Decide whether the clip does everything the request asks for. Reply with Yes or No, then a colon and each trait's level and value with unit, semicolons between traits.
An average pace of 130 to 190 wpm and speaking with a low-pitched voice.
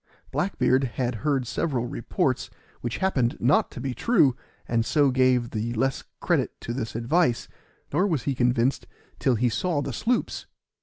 Yes: average, 165 wpm; low, 130 Hz